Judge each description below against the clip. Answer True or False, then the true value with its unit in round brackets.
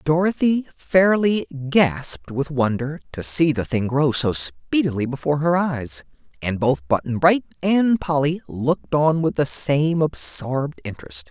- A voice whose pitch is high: False (140 Hz)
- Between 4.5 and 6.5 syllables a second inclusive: False (4.3 syllables/s)